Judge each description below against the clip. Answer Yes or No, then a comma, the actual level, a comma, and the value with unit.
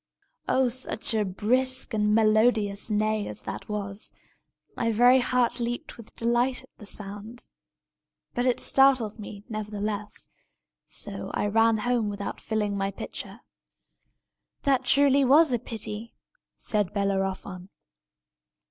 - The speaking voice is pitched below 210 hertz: No, high, 220 Hz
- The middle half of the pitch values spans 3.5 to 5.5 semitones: No, average, 2.9 semitones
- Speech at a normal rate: No, slow, 130 wpm